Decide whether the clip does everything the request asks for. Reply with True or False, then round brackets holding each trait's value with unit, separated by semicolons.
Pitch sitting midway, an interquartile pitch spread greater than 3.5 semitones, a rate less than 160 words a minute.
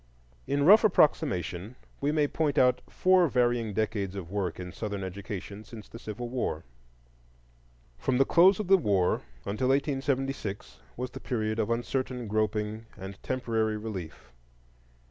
False (115 Hz; 4.8 semitones; 145 wpm)